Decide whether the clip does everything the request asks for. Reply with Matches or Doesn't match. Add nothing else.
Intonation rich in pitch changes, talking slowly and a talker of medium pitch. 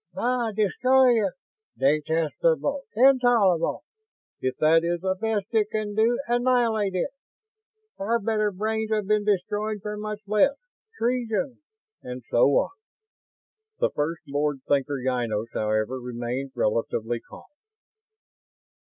Doesn't match